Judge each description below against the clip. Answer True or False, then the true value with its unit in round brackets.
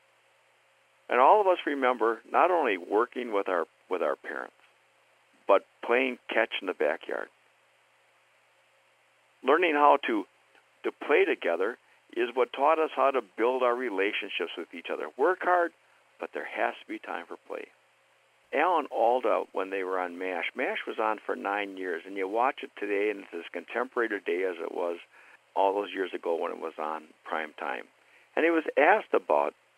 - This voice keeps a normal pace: True (180 wpm)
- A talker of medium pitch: False (125 Hz)